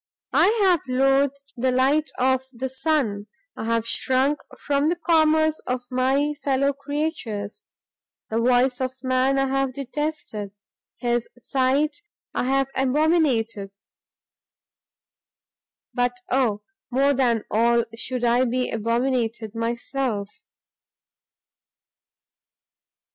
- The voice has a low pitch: No, very high, 260 Hz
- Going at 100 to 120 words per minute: Yes, slow, 105 wpm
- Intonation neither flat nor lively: Yes, average, 3.0 semitones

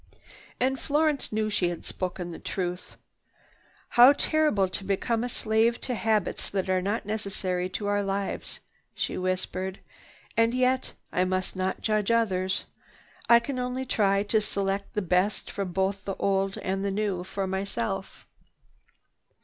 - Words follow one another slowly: No, average, 150 wpm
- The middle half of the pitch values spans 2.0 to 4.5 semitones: Yes, average, 3.1 semitones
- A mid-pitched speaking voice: No, high, 200 Hz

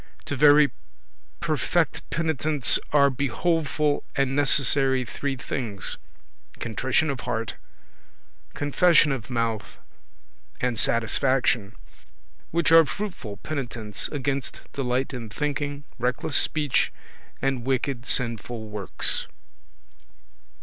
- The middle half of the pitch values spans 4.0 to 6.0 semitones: No, average, 3.3 semitones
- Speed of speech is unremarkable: No, slow, 95 wpm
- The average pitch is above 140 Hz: No, low, 135 Hz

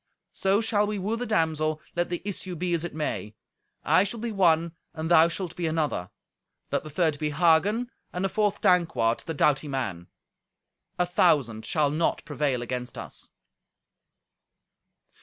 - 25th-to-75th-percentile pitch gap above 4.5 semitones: No, average, 4.2 semitones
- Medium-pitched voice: Yes, medium, 165 Hz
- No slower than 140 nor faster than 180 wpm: Yes, average, 160 wpm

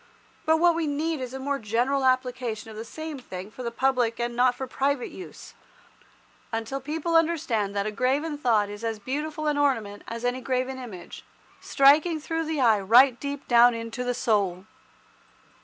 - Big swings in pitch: No, average, 4.1 semitones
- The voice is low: No, very high, 255 Hz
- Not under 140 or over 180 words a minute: Yes, average, 175 wpm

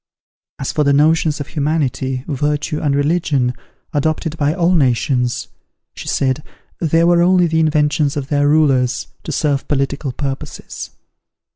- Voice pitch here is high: No, medium, 145 Hz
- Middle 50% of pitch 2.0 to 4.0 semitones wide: Yes, narrow, 2.5 semitones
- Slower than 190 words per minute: Yes, average, 140 wpm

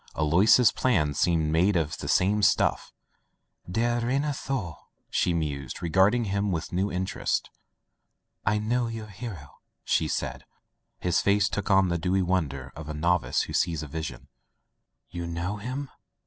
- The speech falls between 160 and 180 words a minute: No, average, 150 wpm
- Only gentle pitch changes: No, average, 4.6 semitones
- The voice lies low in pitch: Yes, very low, 95 Hz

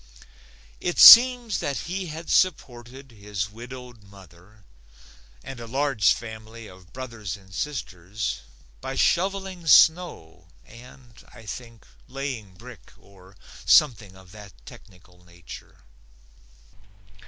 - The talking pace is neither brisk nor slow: No, slow, 110 wpm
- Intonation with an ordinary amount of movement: No, wide, 5.7 semitones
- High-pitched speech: No, low, 115 Hz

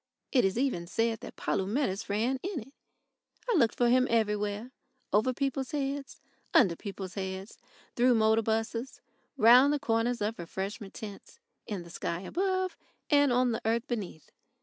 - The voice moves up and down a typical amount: Yes, average, 4.2 semitones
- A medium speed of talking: Yes, average, 155 wpm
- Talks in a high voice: Yes, high, 230 Hz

